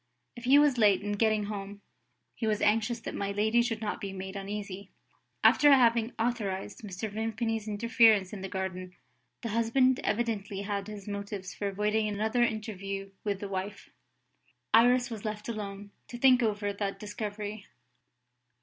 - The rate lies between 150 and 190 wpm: Yes, average, 160 wpm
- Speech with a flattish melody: Yes, narrow, 2.2 semitones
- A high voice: Yes, high, 210 Hz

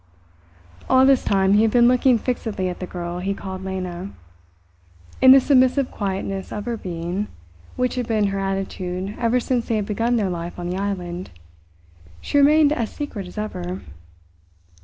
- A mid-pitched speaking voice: No, high, 200 Hz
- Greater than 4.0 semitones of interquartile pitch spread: Yes, average, 4.8 semitones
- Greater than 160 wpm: Yes, average, 170 wpm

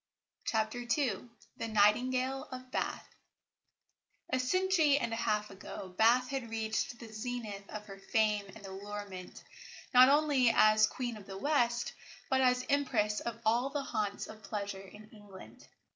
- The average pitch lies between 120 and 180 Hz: No, high, 225 Hz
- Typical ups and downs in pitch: Yes, average, 3.5 semitones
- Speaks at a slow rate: No, average, 150 wpm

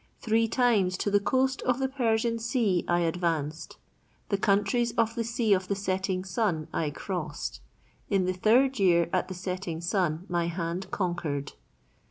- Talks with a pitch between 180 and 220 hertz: Yes, high, 190 Hz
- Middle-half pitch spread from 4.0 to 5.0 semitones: Yes, average, 4.7 semitones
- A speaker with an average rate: Yes, average, 165 wpm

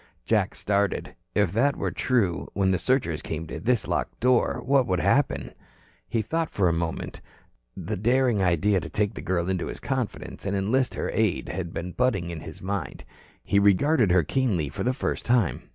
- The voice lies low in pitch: Yes, low, 100 Hz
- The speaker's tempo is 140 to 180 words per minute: No, average, 190 wpm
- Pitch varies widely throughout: Yes, wide, 6.0 semitones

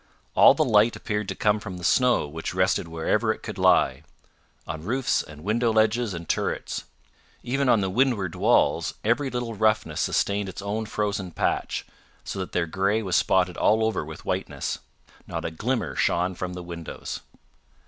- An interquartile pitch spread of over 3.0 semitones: Yes, average, 3.9 semitones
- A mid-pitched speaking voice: No, low, 100 Hz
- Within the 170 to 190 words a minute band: Yes, average, 175 wpm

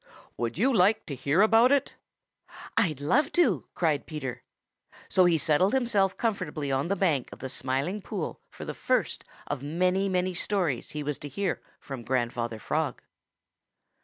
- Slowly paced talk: No, average, 160 wpm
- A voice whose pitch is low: No, medium, 170 Hz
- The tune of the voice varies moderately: No, wide, 6.4 semitones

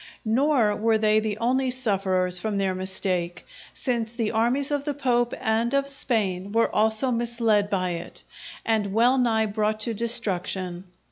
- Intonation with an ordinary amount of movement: Yes, average, 3.3 semitones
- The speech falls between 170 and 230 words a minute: No, average, 155 wpm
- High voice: Yes, high, 220 Hz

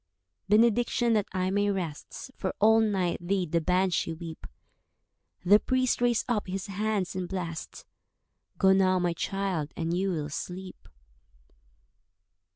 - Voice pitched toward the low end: No, high, 190 Hz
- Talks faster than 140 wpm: No, slow, 135 wpm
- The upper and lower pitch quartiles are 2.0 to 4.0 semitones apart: Yes, average, 2.9 semitones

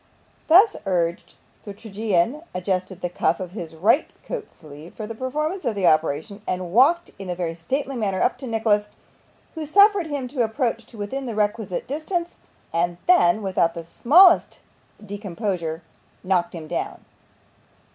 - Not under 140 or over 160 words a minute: Yes, average, 155 wpm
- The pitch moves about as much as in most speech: No, wide, 7.3 semitones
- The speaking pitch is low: No, high, 210 Hz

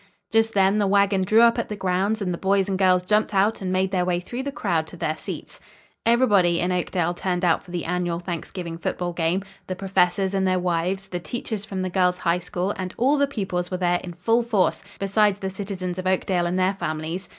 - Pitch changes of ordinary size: No, narrow, 2.0 semitones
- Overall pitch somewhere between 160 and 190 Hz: Yes, medium, 185 Hz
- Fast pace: Yes, fast, 230 wpm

